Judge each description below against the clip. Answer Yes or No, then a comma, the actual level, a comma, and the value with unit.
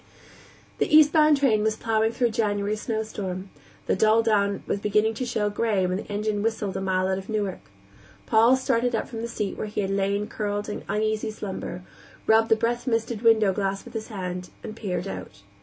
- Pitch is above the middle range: Yes, high, 215 Hz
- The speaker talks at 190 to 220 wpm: Yes, average, 200 wpm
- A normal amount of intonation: No, narrow, 2.2 semitones